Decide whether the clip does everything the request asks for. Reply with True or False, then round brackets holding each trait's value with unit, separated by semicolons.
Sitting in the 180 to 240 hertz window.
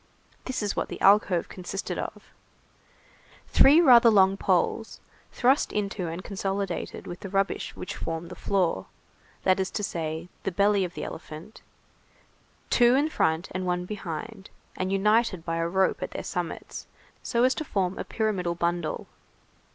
True (190 Hz)